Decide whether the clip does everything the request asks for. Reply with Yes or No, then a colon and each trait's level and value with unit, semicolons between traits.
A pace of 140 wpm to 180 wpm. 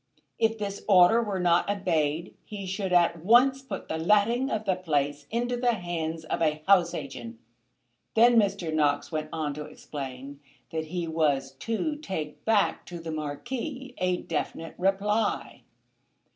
Yes: average, 155 wpm